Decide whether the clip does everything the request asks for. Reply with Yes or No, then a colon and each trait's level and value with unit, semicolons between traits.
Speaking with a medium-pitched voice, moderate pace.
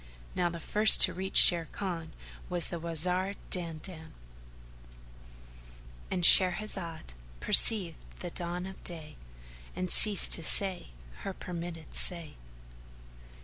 No: medium, 170 Hz; slow, 105 wpm